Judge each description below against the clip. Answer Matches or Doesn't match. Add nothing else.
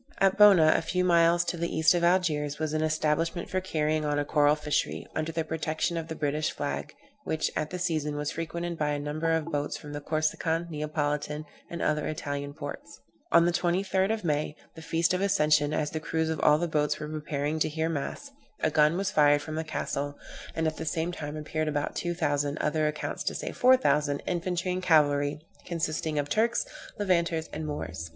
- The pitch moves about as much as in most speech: Doesn't match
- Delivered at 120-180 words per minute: Doesn't match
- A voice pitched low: Doesn't match